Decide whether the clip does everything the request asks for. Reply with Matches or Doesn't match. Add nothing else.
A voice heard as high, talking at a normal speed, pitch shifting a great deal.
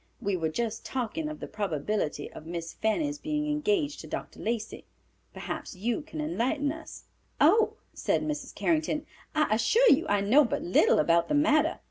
Matches